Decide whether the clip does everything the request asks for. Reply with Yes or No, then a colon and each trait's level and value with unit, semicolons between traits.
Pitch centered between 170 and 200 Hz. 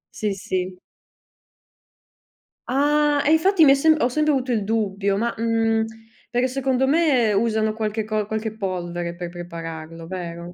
No: high, 220 Hz